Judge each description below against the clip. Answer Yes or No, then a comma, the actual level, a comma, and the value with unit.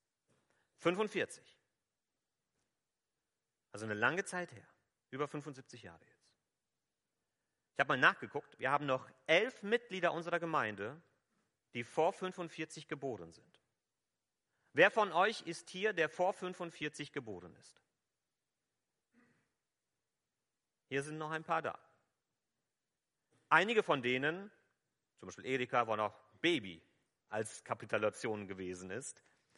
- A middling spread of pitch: No, wide, 6.3 semitones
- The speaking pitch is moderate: Yes, medium, 155 Hz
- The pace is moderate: No, slow, 110 wpm